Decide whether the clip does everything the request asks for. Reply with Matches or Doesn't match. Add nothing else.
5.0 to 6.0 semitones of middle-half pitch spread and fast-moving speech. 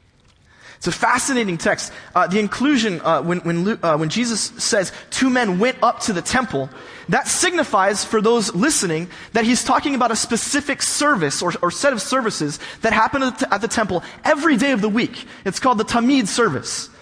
Doesn't match